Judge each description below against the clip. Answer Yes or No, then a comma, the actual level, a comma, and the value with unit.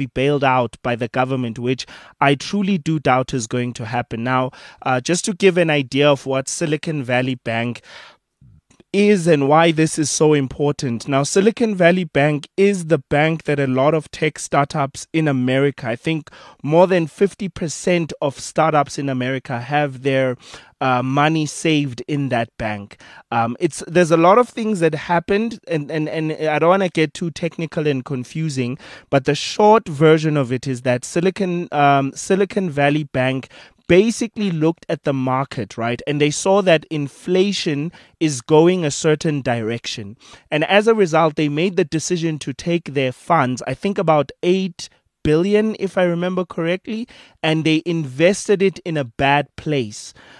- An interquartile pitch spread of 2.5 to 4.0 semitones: No, average, 4.7 semitones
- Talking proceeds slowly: No, average, 175 wpm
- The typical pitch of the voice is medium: Yes, medium, 155 Hz